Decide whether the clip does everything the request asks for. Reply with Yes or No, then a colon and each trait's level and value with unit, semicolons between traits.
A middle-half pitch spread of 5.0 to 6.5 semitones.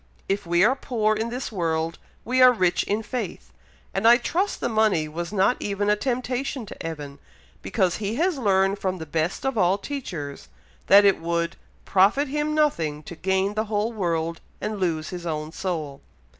Yes: wide, 5.6 semitones